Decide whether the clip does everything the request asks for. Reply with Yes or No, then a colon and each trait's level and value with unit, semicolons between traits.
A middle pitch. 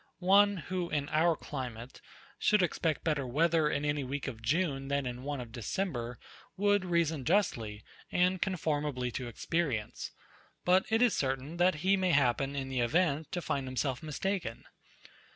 Yes: medium, 150 Hz